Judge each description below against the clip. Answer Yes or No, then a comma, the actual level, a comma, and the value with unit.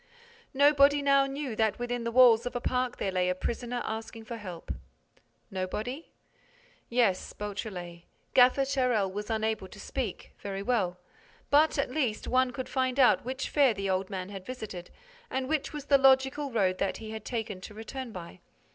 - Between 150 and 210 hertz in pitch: No, high, 235 Hz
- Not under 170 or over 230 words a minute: Yes, average, 175 wpm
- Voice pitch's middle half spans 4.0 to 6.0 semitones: Yes, average, 4.9 semitones